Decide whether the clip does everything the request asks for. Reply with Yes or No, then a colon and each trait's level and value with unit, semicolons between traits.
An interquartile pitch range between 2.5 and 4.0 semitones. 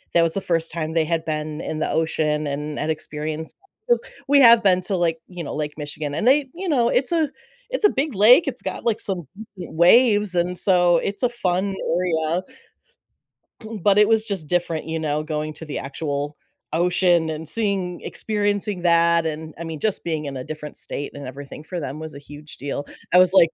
No: average, 4.6 semitones